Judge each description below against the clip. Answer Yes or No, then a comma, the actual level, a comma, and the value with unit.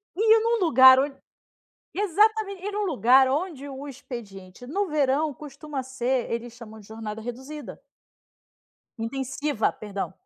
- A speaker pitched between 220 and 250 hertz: No, very high, 270 Hz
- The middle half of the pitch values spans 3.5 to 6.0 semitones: Yes, average, 4.7 semitones